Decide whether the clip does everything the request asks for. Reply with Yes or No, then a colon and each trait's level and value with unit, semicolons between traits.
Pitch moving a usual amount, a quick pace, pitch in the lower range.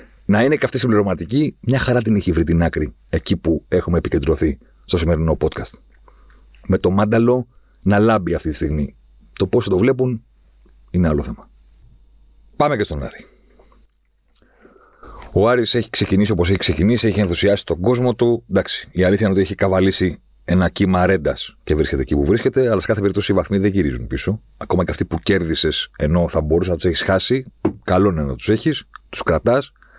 Yes: average, 4.8 semitones; fast, 185 wpm; very low, 95 Hz